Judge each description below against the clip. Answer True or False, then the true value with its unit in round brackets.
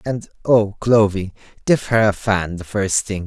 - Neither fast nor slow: True (185 wpm)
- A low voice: True (105 Hz)